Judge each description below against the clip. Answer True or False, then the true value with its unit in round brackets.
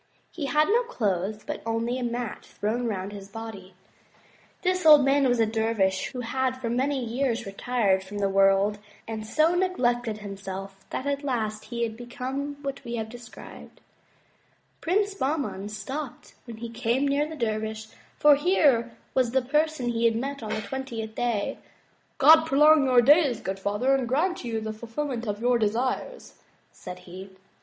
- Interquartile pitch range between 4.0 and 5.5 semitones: True (4.3 semitones)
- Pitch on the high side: True (240 Hz)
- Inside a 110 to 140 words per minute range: False (175 wpm)